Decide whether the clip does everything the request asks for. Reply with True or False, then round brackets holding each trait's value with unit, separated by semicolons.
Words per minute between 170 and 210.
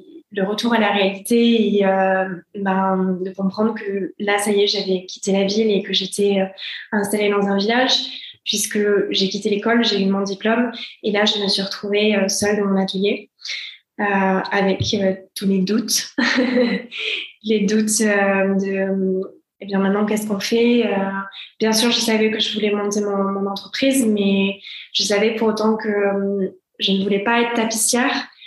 True (190 wpm)